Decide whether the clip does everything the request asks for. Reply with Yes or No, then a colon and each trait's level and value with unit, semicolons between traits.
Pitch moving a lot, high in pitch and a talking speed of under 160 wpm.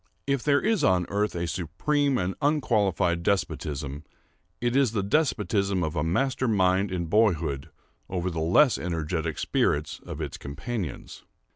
No: wide, 6.5 semitones; very low, 95 Hz; average, 145 wpm